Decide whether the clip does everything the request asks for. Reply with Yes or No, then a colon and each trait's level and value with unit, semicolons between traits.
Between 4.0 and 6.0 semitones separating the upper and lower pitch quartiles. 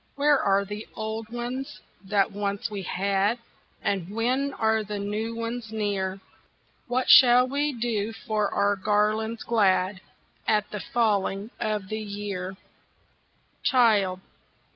No: narrow, 2.5 semitones